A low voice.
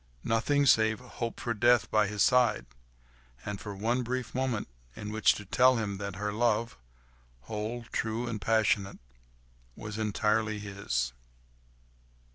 Yes: low, 105 Hz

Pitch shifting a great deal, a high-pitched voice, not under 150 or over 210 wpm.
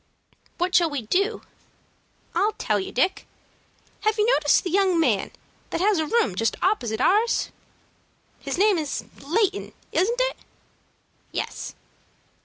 No: wide, 6.0 semitones; very high, 375 Hz; slow, 135 wpm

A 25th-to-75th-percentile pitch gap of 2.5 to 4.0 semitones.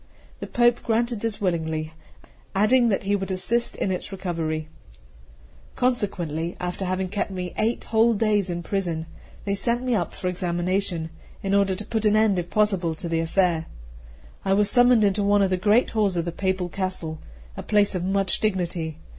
Yes: average, 3.3 semitones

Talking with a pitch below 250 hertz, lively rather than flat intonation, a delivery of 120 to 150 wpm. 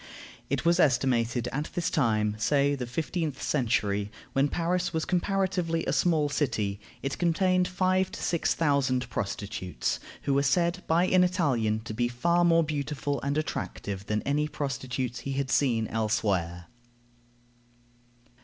Yes: medium, 140 Hz; wide, 6.2 semitones; average, 145 wpm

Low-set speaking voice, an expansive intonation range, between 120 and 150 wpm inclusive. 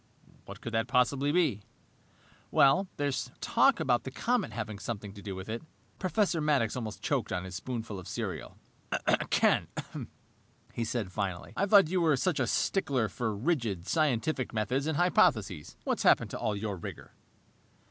No: low, 120 Hz; wide, 6.2 semitones; average, 160 wpm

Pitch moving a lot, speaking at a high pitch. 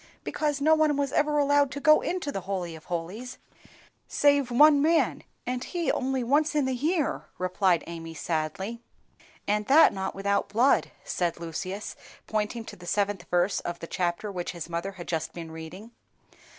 Yes: wide, 8.3 semitones; high, 210 Hz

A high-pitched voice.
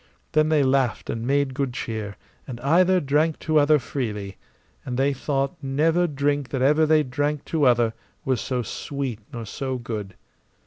No: low, 135 Hz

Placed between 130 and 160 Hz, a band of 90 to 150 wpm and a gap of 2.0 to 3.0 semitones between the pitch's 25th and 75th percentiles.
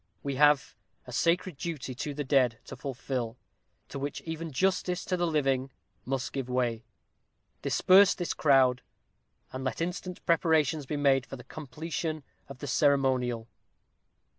No: medium, 140 Hz; average, 145 wpm; average, 4.0 semitones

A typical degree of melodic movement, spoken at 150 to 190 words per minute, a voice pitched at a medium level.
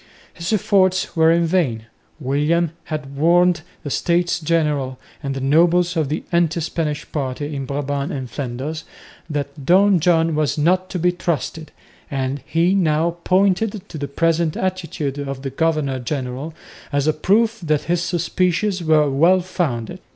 Yes: average, 3.6 semitones; average, 155 wpm; medium, 160 Hz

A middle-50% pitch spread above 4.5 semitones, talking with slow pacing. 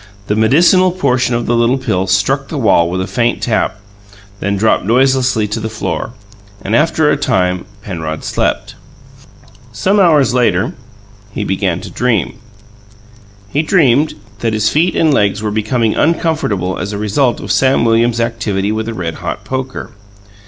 No: average, 4.9 semitones; average, 160 wpm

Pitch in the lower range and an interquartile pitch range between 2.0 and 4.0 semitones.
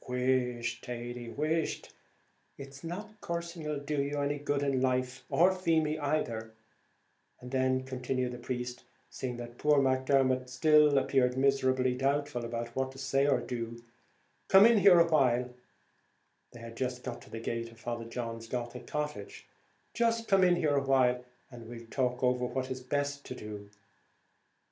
Yes: low, 130 Hz; average, 2.9 semitones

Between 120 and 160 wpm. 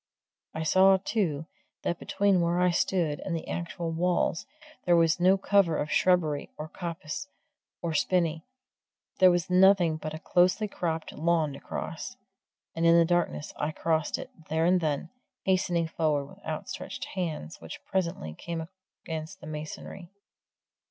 Yes: average, 150 wpm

